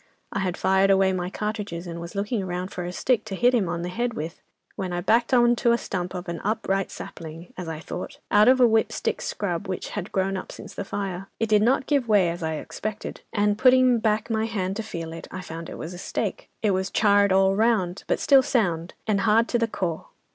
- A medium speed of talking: No, fast, 240 wpm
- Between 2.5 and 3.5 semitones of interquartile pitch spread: No, average, 3.9 semitones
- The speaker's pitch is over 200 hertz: No, high, 195 Hz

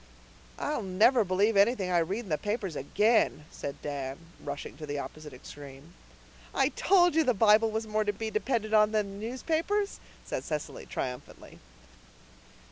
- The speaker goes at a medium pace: Yes, average, 160 wpm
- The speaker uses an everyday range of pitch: No, wide, 6.6 semitones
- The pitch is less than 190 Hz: No, high, 205 Hz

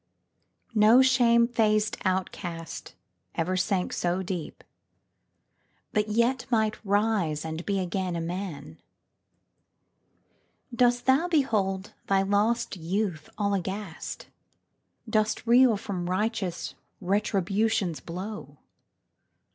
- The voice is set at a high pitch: Yes, high, 200 Hz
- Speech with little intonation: No, average, 3.7 semitones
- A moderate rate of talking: No, slow, 95 wpm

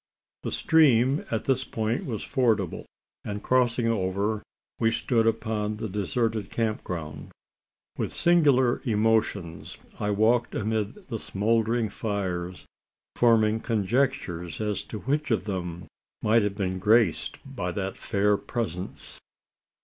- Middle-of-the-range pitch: No, low, 110 Hz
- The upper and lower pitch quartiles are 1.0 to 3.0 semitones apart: Yes, average, 2.7 semitones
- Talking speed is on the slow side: Yes, slow, 125 wpm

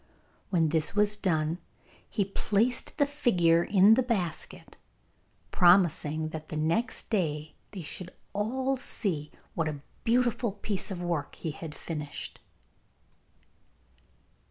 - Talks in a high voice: No, medium, 180 Hz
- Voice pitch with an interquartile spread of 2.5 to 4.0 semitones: No, average, 5.2 semitones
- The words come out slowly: Yes, slow, 120 wpm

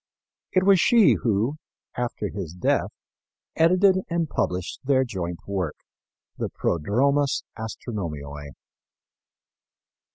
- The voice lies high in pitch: No, low, 110 Hz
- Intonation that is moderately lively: No, wide, 9.0 semitones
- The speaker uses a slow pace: Yes, slow, 95 wpm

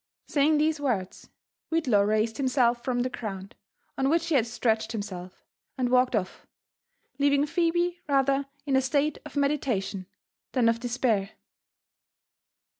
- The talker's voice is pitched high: Yes, very high, 255 Hz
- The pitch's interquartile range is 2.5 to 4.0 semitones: No, average, 4.5 semitones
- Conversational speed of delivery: No, slow, 130 wpm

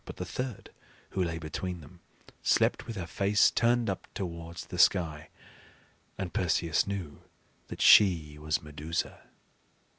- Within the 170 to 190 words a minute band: No, average, 140 wpm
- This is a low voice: Yes, very low, 85 Hz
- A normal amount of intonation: Yes, average, 3.9 semitones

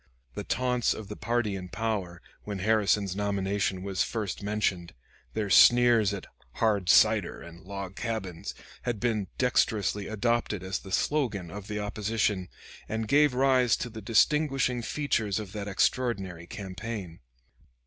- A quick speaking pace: No, average, 140 wpm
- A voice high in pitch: No, low, 105 Hz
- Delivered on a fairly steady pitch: No, average, 3.3 semitones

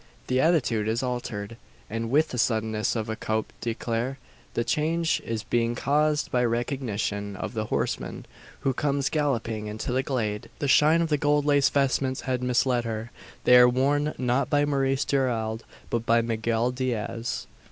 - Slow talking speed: No, average, 165 wpm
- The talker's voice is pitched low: Yes, low, 125 Hz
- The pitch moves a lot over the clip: No, average, 3.5 semitones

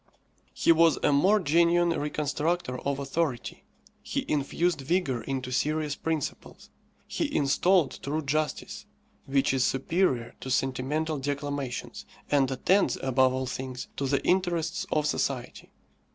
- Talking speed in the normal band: No, slow, 125 wpm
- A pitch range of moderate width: Yes, average, 3.7 semitones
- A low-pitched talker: No, medium, 145 Hz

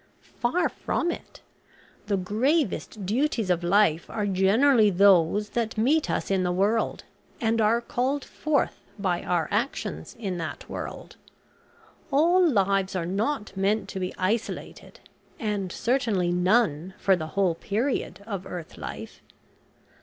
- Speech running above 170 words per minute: No, slow, 135 wpm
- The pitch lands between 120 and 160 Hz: No, high, 205 Hz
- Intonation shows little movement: No, average, 4.2 semitones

